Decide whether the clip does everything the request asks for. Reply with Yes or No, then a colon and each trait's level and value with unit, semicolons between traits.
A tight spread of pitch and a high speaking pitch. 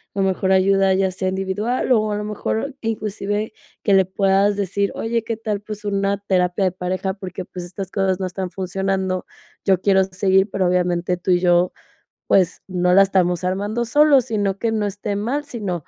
Yes: narrow, 2.1 semitones; high, 195 Hz